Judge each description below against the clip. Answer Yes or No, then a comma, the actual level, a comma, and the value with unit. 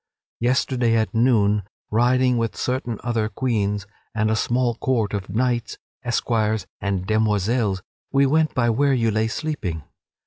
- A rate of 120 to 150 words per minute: Yes, average, 140 wpm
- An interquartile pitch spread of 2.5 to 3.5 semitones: Yes, average, 2.9 semitones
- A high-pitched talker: No, low, 115 Hz